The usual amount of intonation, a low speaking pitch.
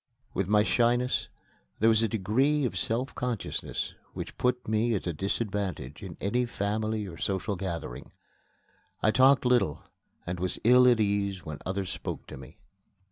Yes: average, 4.2 semitones; low, 105 Hz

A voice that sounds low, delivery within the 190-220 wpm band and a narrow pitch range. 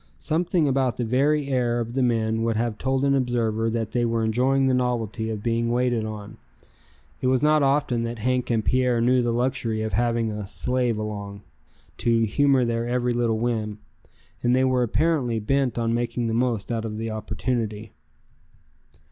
No: low, 120 Hz; average, 180 wpm; narrow, 2.3 semitones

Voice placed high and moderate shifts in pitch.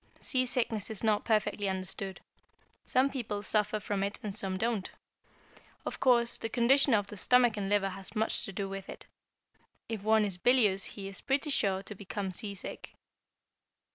Yes: high, 210 Hz; average, 3.2 semitones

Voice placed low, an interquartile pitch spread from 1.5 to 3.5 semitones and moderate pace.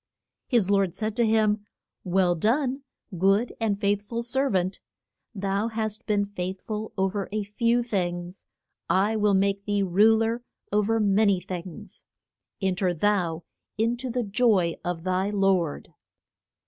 No: high, 205 Hz; average, 2.8 semitones; average, 160 wpm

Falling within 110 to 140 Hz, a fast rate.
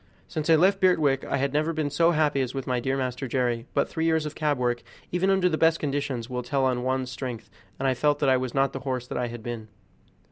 Yes: low, 135 Hz; fast, 260 wpm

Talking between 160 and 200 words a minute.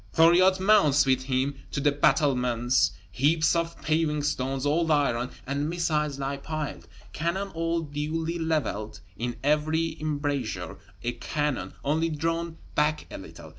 No: slow, 135 wpm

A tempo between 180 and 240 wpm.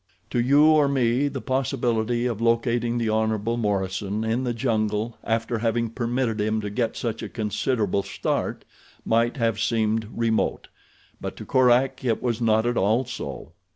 No: average, 160 wpm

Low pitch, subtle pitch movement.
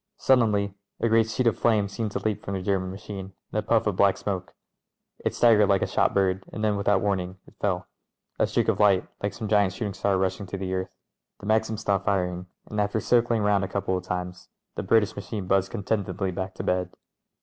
Yes: low, 100 Hz; narrow, 2.2 semitones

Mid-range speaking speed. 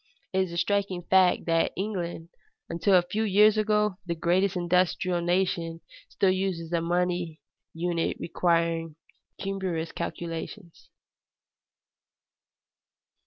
No: slow, 110 wpm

